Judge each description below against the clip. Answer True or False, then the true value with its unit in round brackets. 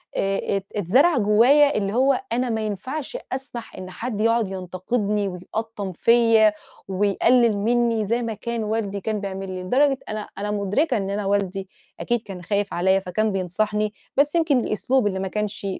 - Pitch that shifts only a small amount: False (3.4 semitones)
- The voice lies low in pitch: False (210 Hz)